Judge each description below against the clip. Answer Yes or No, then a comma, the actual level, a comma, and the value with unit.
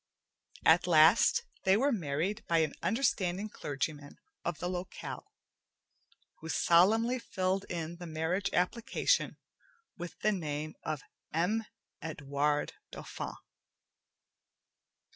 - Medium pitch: Yes, medium, 175 Hz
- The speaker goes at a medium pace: No, slow, 105 wpm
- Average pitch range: Yes, average, 4.2 semitones